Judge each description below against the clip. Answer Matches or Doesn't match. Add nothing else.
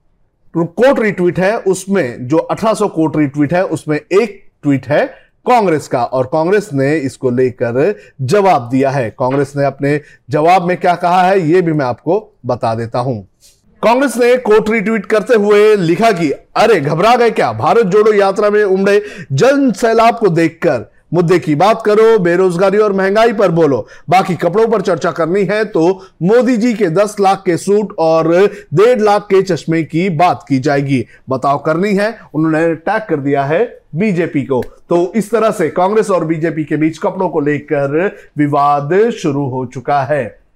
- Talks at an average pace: Matches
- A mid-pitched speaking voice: Matches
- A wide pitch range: Matches